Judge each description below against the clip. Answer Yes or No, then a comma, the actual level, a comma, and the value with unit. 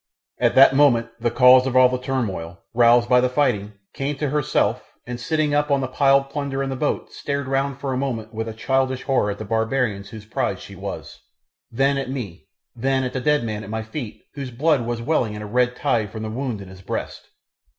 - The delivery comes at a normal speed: No, fast, 225 wpm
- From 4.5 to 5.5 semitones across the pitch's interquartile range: No, average, 3.4 semitones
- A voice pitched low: Yes, low, 125 Hz